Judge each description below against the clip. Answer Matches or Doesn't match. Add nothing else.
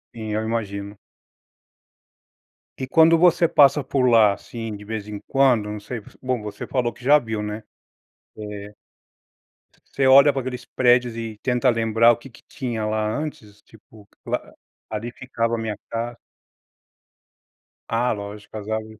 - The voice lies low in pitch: Matches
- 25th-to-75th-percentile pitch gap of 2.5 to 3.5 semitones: Matches